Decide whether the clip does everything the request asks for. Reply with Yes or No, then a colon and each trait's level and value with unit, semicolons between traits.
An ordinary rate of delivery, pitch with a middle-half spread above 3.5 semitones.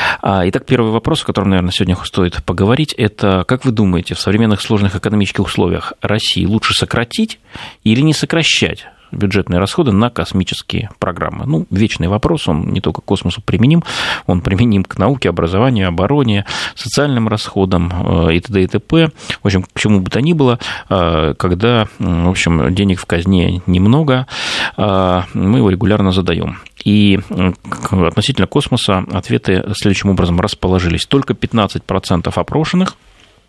Yes: average, 140 wpm; average, 4.5 semitones